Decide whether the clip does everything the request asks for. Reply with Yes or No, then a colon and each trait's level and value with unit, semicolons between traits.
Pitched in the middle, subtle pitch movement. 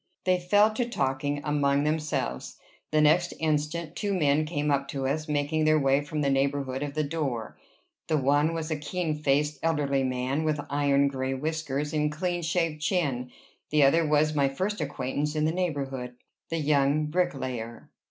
Yes: medium, 150 Hz; narrow, 2.3 semitones